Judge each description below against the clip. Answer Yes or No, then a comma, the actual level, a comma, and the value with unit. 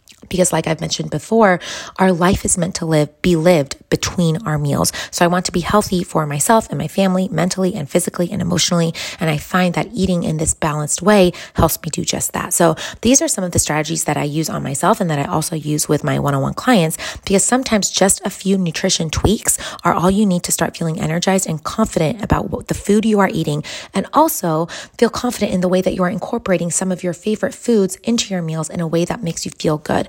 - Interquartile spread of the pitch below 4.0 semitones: Yes, average, 3.2 semitones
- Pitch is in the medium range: Yes, medium, 180 Hz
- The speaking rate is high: Yes, fast, 240 wpm